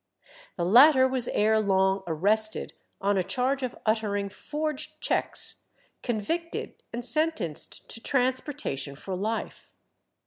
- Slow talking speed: Yes, slow, 115 wpm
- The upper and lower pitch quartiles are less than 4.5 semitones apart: No, average, 5.2 semitones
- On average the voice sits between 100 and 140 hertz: No, high, 225 Hz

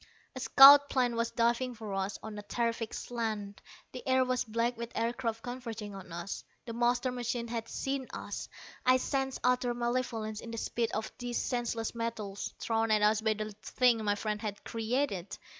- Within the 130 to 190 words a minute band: Yes, average, 180 wpm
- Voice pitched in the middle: No, high, 230 Hz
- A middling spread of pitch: No, narrow, 2.3 semitones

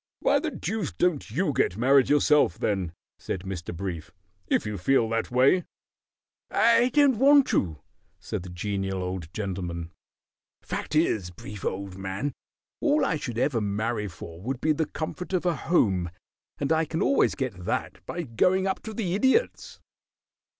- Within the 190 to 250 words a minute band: No, average, 165 wpm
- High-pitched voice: No, low, 120 Hz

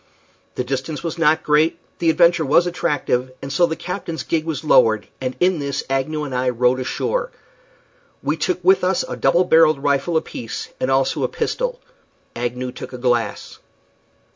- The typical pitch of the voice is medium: Yes, medium, 150 Hz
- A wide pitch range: No, average, 4.8 semitones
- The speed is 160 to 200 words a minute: Yes, average, 170 wpm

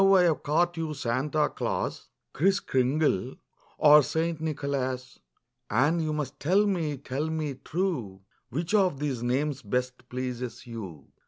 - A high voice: No, medium, 145 Hz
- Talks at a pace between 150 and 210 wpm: No, average, 140 wpm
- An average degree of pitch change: Yes, average, 4.0 semitones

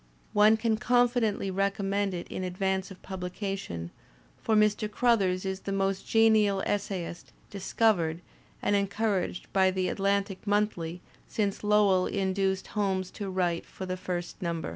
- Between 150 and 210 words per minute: No, average, 140 wpm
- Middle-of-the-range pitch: No, high, 195 Hz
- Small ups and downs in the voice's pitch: Yes, narrow, 2.0 semitones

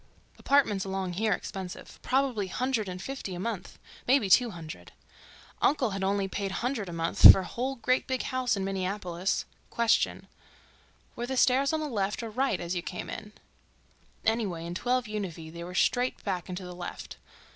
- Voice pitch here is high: Yes, high, 200 Hz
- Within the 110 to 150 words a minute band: No, average, 165 wpm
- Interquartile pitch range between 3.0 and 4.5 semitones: No, wide, 5.4 semitones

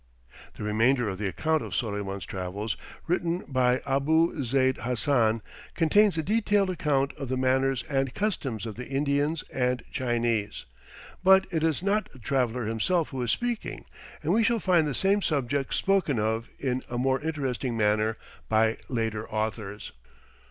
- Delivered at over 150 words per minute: Yes, average, 160 wpm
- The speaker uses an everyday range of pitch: No, wide, 6.0 semitones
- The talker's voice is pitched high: No, low, 130 Hz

